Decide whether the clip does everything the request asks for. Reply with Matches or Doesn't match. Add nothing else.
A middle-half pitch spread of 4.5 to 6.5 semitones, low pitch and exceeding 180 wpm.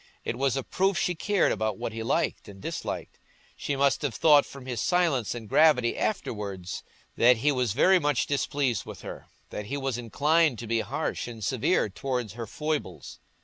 Matches